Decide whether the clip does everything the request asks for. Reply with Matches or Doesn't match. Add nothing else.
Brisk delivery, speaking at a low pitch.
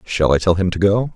Matches